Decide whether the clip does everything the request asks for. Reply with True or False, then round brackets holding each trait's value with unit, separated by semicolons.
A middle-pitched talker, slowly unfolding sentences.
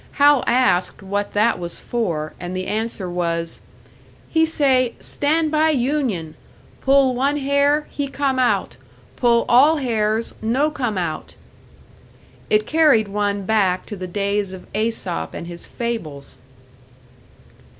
False (225 Hz; 130 wpm)